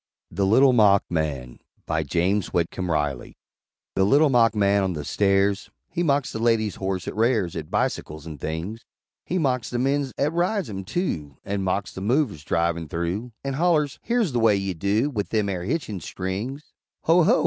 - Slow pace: No, average, 190 wpm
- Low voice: Yes, low, 100 Hz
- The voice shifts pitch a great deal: Yes, wide, 7.0 semitones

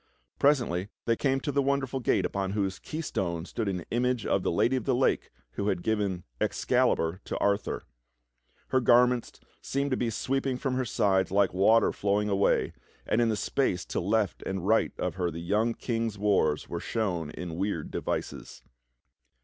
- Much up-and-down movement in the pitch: No, average, 4.6 semitones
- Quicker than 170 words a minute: Yes, average, 180 wpm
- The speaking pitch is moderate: No, low, 105 Hz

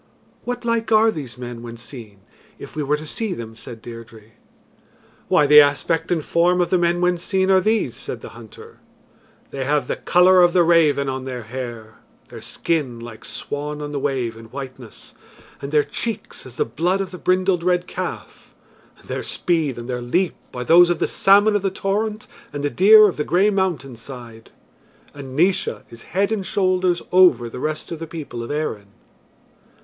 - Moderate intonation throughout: No, wide, 6.6 semitones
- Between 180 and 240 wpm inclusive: Yes, average, 195 wpm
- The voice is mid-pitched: Yes, medium, 155 Hz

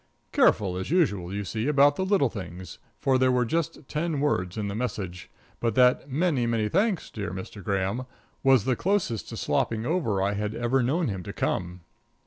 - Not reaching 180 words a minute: No, average, 190 wpm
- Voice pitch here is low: Yes, low, 120 Hz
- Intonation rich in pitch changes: Yes, wide, 6.3 semitones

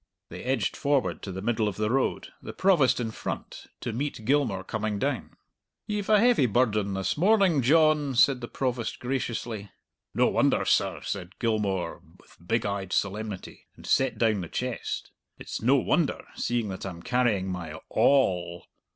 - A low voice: Yes, low, 115 Hz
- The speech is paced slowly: No, average, 170 wpm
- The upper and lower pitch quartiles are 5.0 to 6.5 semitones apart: Yes, average, 5.3 semitones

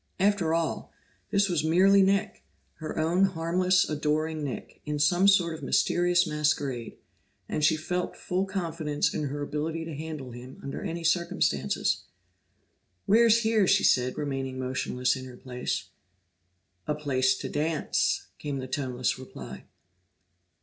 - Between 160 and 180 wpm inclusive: No, average, 140 wpm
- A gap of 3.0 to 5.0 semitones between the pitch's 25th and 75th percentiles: Yes, average, 4.3 semitones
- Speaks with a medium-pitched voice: Yes, medium, 155 Hz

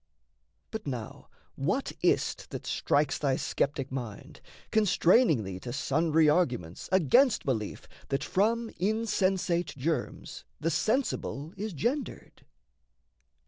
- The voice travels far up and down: Yes, wide, 7.7 semitones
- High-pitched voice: No, medium, 160 Hz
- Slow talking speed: Yes, slow, 105 wpm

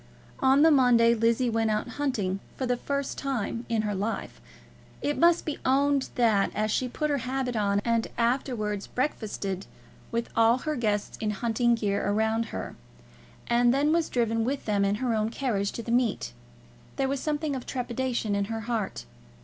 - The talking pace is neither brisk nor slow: Yes, average, 180 wpm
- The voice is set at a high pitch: Yes, high, 235 Hz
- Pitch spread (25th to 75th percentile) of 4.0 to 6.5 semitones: No, average, 3.5 semitones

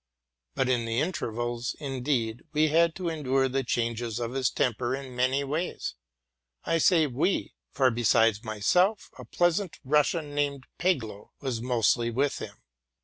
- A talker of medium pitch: No, low, 130 Hz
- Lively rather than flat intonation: No, average, 4.2 semitones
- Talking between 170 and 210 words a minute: No, average, 145 wpm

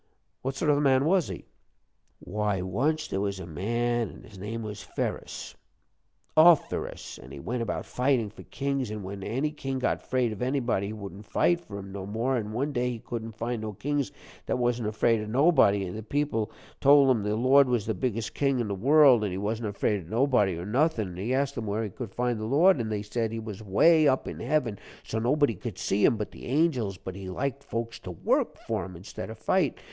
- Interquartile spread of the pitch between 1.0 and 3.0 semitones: No, average, 4.6 semitones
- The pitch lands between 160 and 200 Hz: No, low, 115 Hz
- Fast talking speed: Yes, fast, 230 wpm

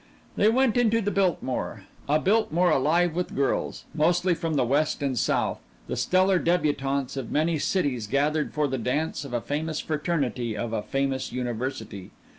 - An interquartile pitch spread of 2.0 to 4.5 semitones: No, average, 5.0 semitones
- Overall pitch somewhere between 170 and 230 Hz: No, medium, 150 Hz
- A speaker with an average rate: Yes, average, 165 wpm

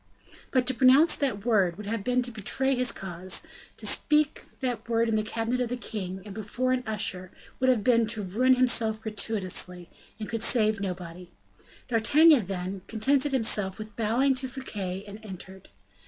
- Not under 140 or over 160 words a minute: No, average, 175 wpm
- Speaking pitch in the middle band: No, high, 220 Hz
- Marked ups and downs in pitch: No, average, 4.2 semitones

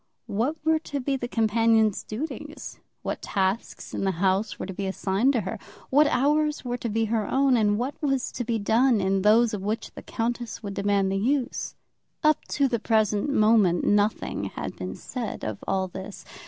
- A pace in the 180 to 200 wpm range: Yes, average, 195 wpm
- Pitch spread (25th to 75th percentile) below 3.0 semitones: No, average, 4.0 semitones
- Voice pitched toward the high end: Yes, high, 225 Hz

